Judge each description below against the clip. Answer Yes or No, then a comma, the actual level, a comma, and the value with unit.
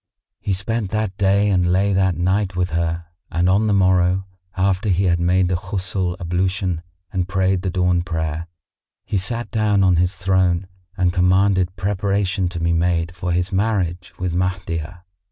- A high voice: No, very low, 90 Hz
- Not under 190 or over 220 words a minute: No, average, 170 wpm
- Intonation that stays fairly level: Yes, narrow, 1.7 semitones